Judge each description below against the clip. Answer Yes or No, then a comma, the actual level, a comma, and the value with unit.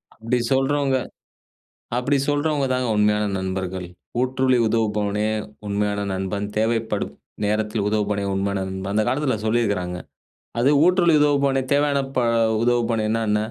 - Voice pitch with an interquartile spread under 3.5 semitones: No, average, 4.6 semitones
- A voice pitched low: Yes, low, 110 Hz